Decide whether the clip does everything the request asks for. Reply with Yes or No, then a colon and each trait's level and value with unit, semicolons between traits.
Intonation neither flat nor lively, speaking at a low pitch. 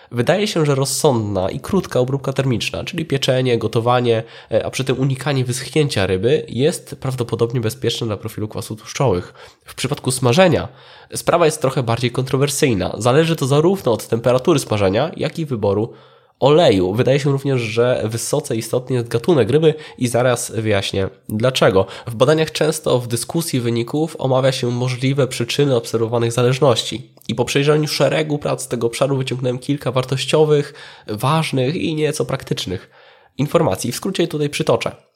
Yes: average, 3.8 semitones; low, 130 Hz